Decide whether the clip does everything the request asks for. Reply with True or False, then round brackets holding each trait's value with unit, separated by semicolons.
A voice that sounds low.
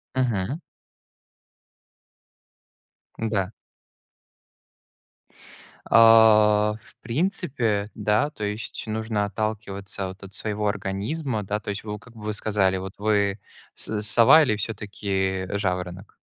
True (105 Hz)